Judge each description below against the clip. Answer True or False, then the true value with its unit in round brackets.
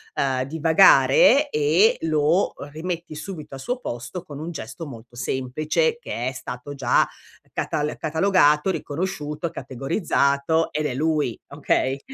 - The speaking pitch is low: False (150 Hz)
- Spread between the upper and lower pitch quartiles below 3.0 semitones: False (3.7 semitones)